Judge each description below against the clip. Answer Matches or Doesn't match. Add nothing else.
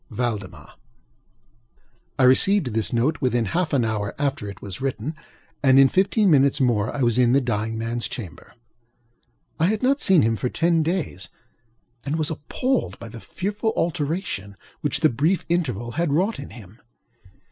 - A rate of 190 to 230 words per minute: Doesn't match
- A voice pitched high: Doesn't match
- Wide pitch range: Matches